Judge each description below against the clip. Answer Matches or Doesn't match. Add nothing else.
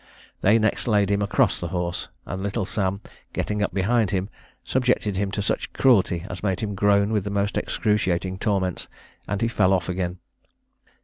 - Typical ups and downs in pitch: Doesn't match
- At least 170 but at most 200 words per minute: Matches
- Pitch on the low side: Matches